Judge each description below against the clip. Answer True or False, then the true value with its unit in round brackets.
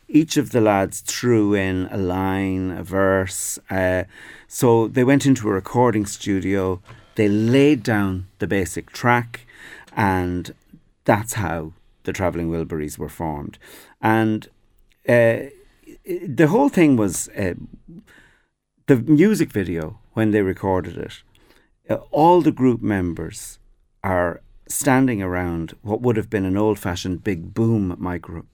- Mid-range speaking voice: False (105 Hz)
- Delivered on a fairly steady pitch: False (3.9 semitones)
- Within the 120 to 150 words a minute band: True (135 wpm)